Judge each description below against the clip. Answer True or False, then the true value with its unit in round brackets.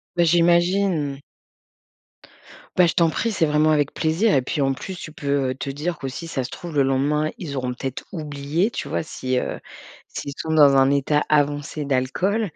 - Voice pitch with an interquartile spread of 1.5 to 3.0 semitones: False (3.5 semitones)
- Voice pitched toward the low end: False (150 Hz)